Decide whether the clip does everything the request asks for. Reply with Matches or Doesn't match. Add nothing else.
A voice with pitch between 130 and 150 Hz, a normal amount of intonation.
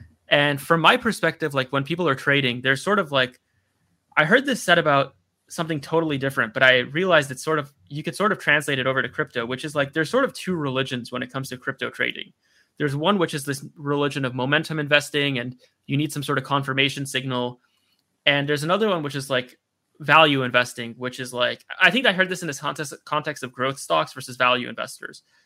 Matches